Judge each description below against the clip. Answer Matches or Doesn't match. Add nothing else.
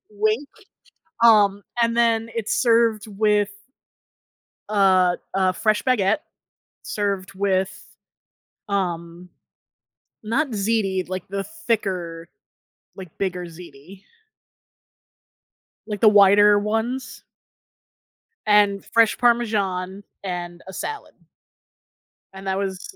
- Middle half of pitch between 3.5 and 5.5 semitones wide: Doesn't match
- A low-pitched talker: Doesn't match